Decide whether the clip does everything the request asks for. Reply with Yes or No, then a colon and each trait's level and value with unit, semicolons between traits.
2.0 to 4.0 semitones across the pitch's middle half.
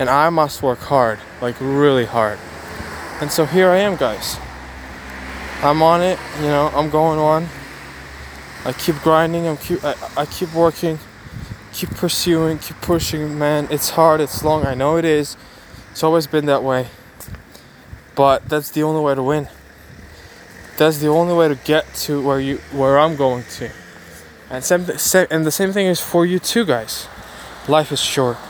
No: average, 5.3 semitones